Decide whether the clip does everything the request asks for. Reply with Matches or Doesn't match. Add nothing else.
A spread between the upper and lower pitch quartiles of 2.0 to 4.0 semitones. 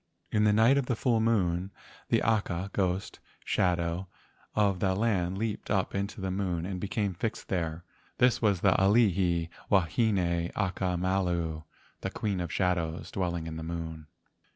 Matches